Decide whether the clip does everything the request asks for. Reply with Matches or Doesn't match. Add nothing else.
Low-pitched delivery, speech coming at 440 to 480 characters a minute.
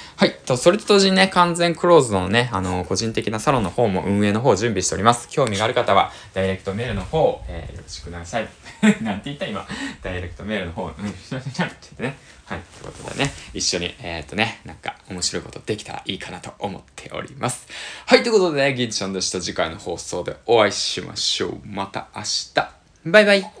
Matches